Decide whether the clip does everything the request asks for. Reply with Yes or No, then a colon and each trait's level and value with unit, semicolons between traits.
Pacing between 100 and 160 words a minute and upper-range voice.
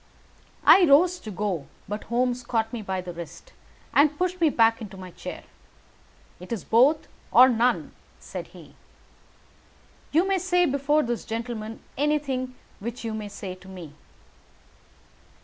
Yes: average, 150 wpm; high, 235 Hz